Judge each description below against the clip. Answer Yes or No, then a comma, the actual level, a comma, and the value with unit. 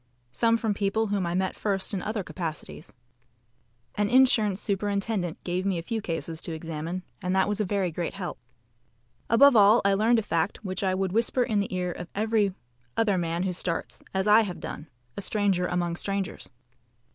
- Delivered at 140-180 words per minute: No, average, 190 wpm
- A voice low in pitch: No, high, 195 Hz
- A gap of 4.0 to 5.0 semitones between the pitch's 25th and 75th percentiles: No, average, 2.9 semitones